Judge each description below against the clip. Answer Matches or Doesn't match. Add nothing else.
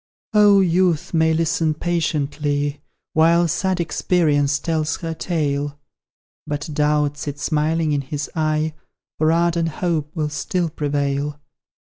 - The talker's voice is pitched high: Doesn't match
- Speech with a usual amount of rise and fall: Doesn't match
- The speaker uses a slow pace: Matches